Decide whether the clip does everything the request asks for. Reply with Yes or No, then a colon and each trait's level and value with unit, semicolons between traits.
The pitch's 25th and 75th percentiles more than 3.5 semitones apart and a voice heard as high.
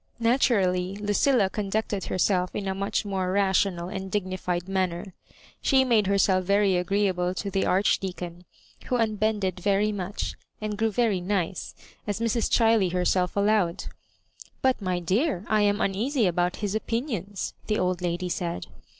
No: average, 2.7 semitones; high, 195 Hz